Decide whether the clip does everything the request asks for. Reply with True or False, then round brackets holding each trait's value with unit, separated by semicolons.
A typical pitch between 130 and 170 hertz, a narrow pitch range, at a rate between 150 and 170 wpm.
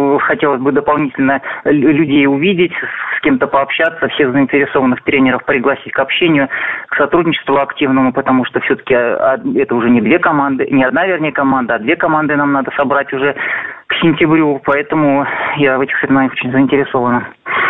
True (140 Hz; 1.8 semitones; 155 wpm)